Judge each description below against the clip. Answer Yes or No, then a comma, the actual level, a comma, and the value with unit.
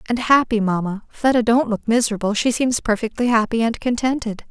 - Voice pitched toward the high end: Yes, high, 230 Hz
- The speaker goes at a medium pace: Yes, average, 145 wpm